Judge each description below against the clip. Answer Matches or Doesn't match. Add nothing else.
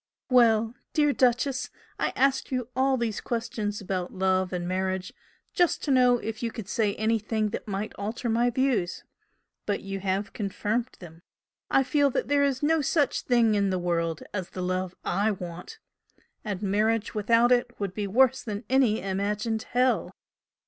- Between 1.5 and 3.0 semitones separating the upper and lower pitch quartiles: Doesn't match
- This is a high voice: Matches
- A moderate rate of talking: Matches